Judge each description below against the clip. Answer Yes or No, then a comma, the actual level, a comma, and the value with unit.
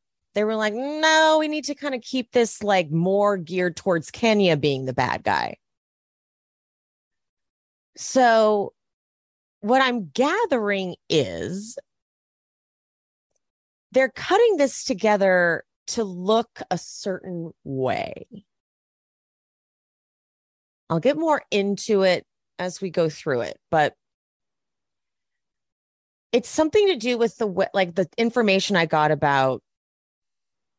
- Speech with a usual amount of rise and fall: No, wide, 6.3 semitones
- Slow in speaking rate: Yes, slow, 110 wpm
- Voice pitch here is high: Yes, high, 200 Hz